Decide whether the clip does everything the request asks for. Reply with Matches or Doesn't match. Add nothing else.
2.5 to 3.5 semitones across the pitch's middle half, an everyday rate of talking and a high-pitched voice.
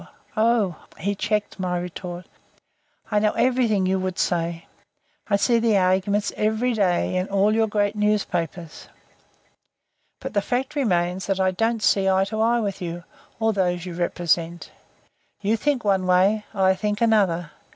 Matches